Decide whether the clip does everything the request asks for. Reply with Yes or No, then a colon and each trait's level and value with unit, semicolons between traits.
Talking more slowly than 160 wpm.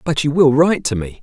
No: fast, 295 wpm